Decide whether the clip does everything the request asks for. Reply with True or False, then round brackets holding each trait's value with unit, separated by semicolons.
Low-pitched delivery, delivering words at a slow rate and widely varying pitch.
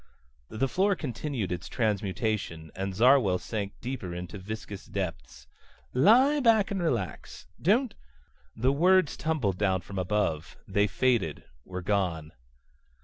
True (105 Hz; 130 wpm; 7.2 semitones)